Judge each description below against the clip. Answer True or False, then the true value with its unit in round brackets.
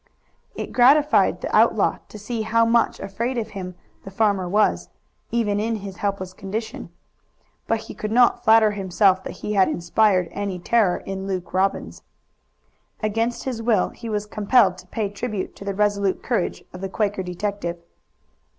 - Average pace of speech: True (165 wpm)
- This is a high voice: True (205 Hz)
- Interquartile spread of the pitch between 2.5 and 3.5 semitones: True (2.8 semitones)